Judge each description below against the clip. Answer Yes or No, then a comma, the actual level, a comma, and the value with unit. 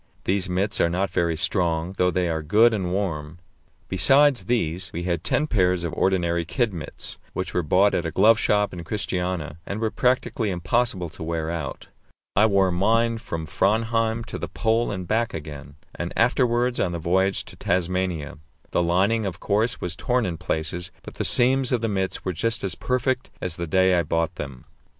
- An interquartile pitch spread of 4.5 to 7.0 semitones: Yes, average, 4.8 semitones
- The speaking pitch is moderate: No, very low, 95 Hz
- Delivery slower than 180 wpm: No, average, 190 wpm